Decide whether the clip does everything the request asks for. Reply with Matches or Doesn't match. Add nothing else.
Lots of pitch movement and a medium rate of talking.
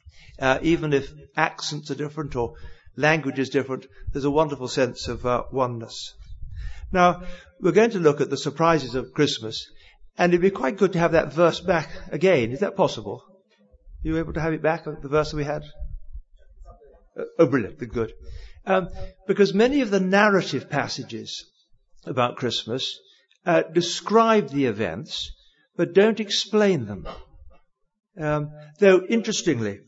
Matches